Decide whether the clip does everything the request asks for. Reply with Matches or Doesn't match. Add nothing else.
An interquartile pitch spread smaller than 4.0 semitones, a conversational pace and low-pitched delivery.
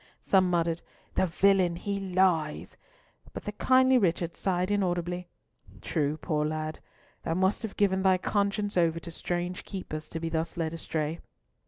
Doesn't match